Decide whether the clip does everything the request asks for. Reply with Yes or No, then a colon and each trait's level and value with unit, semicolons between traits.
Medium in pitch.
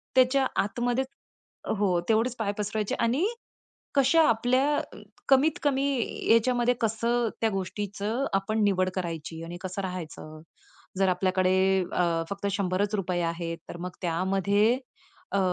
No: high, 205 Hz